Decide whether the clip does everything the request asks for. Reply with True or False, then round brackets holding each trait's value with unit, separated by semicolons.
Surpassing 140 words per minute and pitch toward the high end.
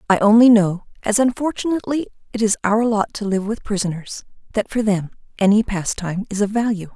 True (165 wpm; 210 Hz)